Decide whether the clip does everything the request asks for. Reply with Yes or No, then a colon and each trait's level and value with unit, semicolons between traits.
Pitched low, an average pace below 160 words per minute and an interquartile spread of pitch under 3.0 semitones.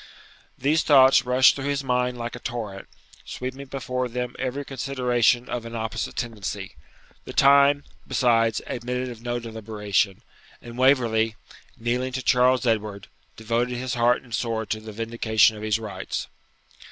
Yes: low, 120 Hz; average, 150 wpm; narrow, 2.4 semitones